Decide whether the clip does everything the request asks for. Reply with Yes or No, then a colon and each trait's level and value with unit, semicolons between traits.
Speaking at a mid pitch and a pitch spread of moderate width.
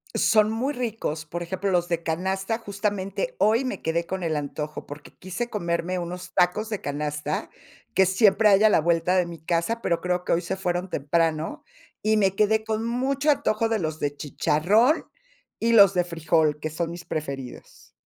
Yes: medium, 180 Hz; average, 4.7 semitones